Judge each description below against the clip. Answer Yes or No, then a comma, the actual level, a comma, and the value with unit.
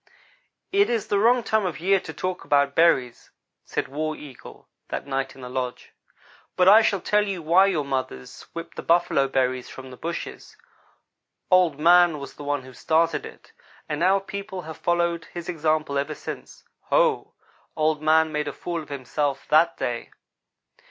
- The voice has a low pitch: No, medium, 160 Hz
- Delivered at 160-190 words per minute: Yes, average, 175 wpm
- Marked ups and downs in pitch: No, average, 4.3 semitones